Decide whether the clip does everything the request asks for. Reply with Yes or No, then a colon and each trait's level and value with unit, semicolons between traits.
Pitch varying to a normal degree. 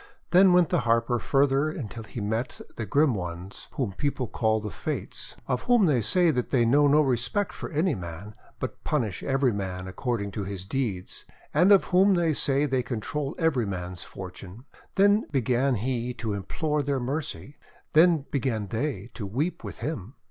No: wide, 5.9 semitones